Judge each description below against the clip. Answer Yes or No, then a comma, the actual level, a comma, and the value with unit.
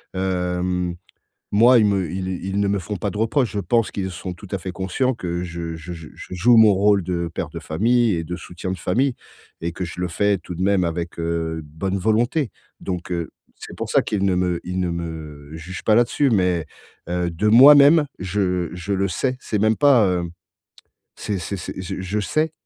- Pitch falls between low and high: No, very low, 95 Hz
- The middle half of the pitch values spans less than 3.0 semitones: No, average, 3.3 semitones